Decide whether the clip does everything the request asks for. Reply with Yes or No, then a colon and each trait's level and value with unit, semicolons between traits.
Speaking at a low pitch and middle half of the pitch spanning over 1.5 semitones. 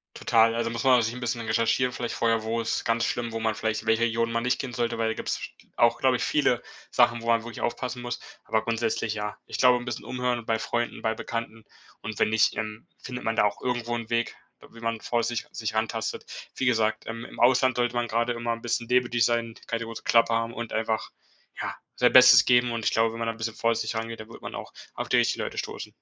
No: low, 115 Hz; narrow, 1.0 semitones